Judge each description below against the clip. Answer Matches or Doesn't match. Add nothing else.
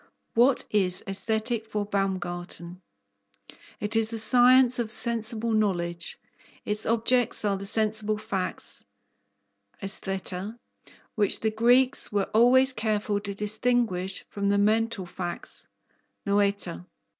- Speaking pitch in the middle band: Doesn't match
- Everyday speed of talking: Doesn't match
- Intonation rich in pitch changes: Doesn't match